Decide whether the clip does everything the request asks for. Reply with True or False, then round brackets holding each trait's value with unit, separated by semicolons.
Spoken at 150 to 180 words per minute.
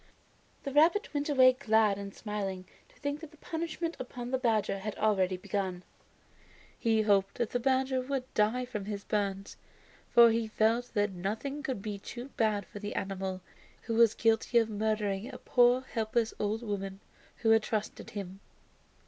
True (170 wpm)